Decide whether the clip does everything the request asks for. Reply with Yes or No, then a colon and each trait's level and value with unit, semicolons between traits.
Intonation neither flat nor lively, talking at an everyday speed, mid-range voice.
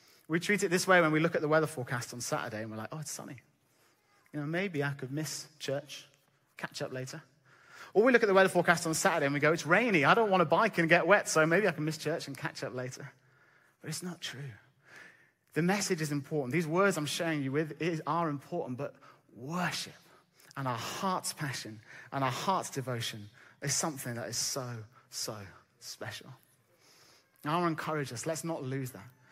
No: average, 4.4 semitones; fast, 210 wpm; medium, 150 Hz